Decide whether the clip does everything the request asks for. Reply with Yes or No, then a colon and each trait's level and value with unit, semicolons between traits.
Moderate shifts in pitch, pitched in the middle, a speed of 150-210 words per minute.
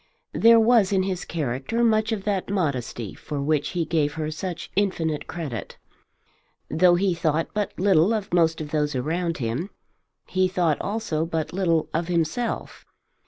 Yes: average, 4.0 semitones; medium, 170 Hz; average, 160 wpm